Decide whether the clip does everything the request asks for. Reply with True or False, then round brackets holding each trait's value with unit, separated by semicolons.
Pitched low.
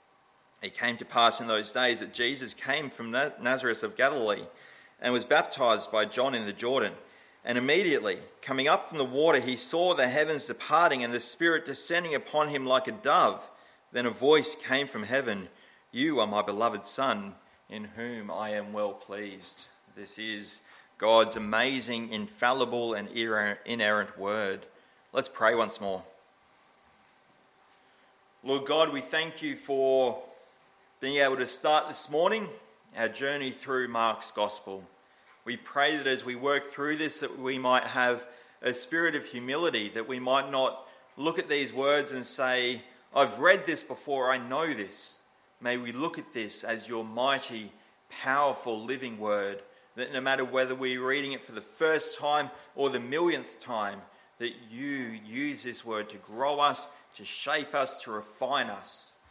True (130 Hz)